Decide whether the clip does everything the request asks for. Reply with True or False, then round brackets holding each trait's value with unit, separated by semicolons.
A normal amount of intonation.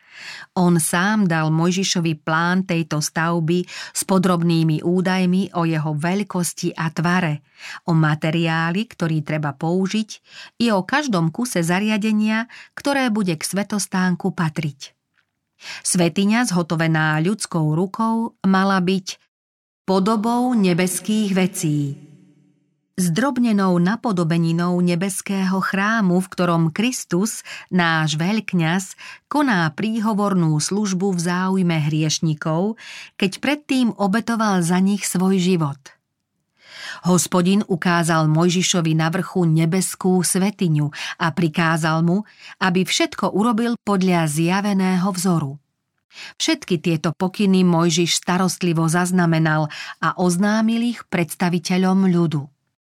True (3.2 semitones)